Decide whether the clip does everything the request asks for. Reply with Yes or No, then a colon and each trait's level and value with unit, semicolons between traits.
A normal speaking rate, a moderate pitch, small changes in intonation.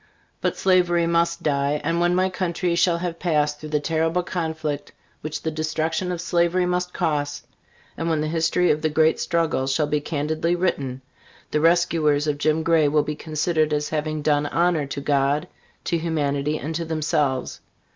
Yes: average, 175 wpm; medium, 155 Hz; narrow, 2.3 semitones